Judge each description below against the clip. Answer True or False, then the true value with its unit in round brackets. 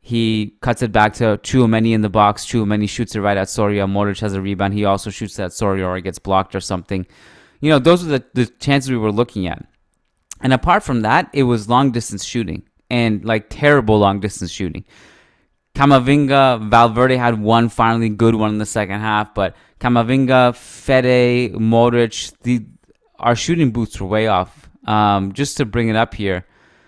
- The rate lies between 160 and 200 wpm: True (190 wpm)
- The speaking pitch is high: False (110 Hz)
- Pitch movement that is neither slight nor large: True (3.3 semitones)